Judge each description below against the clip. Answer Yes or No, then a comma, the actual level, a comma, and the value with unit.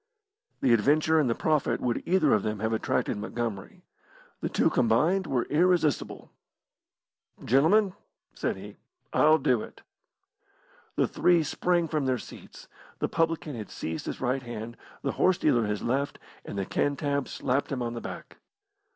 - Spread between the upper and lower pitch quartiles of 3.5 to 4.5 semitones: No, average, 5.3 semitones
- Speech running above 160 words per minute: No, average, 155 wpm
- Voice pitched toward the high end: No, low, 135 Hz